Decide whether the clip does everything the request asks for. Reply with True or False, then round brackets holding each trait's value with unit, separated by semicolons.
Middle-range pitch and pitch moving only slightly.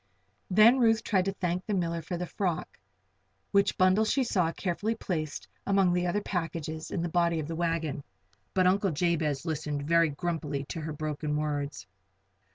False (170 Hz; 3.3 semitones)